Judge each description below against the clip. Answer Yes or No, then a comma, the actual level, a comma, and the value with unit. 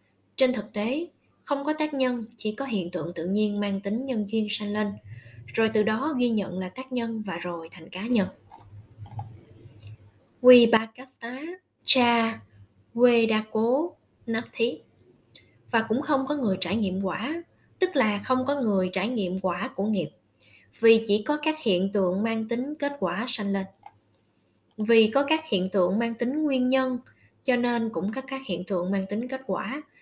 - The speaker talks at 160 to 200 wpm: Yes, average, 180 wpm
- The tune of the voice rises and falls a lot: Yes, wide, 5.7 semitones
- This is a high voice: Yes, high, 215 Hz